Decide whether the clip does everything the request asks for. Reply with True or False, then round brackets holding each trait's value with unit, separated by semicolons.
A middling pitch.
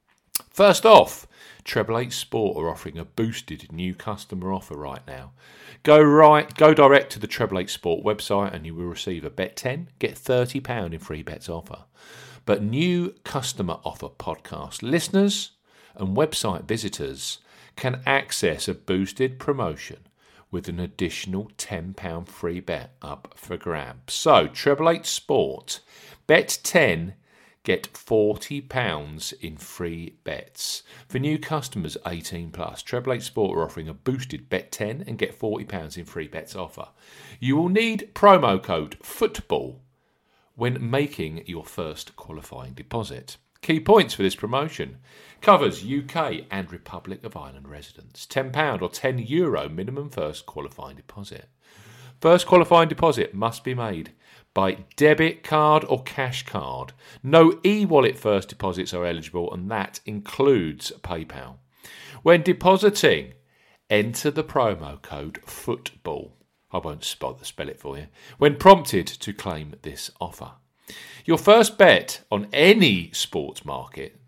False (110 Hz)